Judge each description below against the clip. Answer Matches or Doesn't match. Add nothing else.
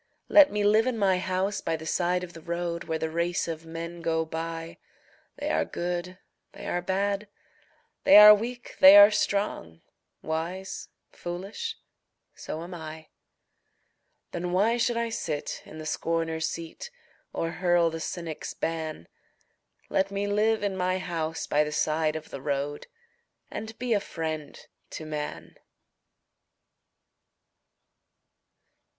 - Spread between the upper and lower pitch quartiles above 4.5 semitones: Doesn't match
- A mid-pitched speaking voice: Matches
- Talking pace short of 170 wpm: Matches